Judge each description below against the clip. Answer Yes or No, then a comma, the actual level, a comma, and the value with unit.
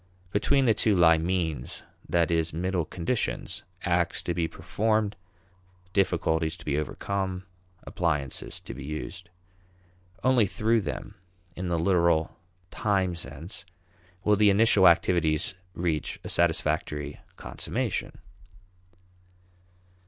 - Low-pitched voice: Yes, very low, 85 Hz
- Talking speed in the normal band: No, slow, 110 wpm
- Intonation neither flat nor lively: Yes, average, 3.5 semitones